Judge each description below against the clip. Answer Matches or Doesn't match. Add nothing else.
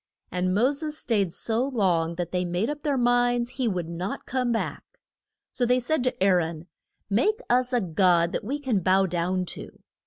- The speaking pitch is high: Matches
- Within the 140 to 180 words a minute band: Doesn't match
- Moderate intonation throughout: Doesn't match